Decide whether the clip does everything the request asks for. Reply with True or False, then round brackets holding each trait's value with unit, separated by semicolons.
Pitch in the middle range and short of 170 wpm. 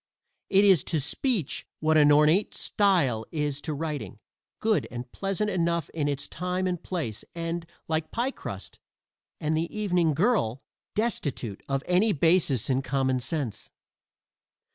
True (160 Hz; 140 wpm)